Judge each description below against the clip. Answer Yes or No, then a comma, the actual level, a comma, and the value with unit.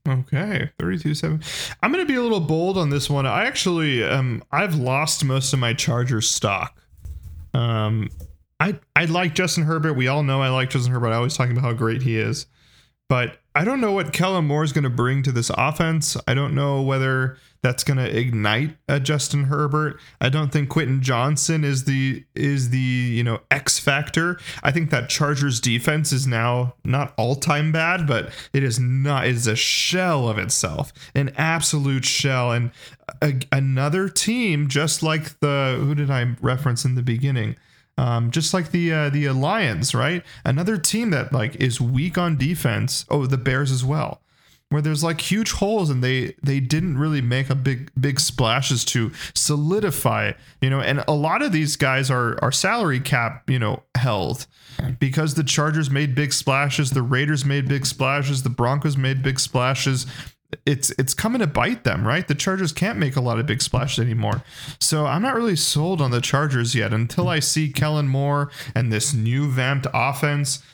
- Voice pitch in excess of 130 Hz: Yes, medium, 140 Hz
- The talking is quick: No, average, 190 wpm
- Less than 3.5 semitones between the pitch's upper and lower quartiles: Yes, average, 3.1 semitones